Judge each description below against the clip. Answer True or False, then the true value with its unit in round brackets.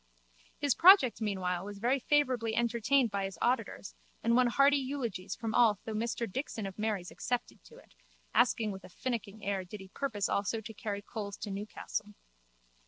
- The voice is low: False (220 Hz)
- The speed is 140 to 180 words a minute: True (175 wpm)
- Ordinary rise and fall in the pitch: True (3.6 semitones)